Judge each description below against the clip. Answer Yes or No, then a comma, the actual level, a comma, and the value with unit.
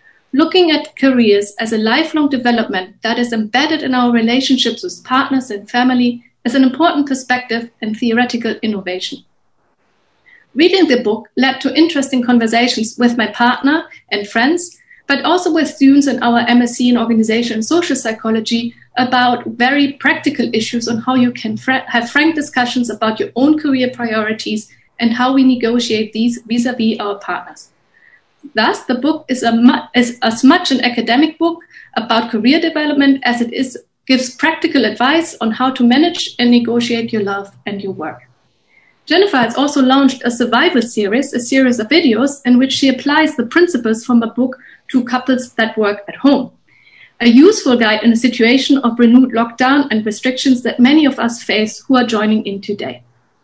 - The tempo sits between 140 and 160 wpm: No, average, 170 wpm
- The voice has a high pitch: Yes, high, 245 Hz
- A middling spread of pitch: Yes, average, 3.2 semitones